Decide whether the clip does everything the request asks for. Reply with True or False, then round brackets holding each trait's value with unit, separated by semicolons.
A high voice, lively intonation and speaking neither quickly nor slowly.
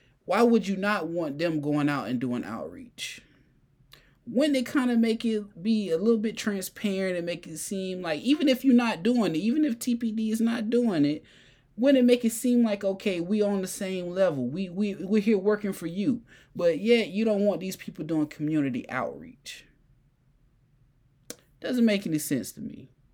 True (200 Hz; 6.7 semitones; 195 wpm)